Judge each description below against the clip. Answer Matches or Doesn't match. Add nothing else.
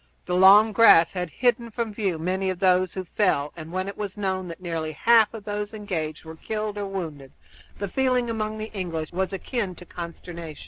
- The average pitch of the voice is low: Doesn't match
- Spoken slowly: Doesn't match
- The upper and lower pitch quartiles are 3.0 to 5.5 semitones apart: Matches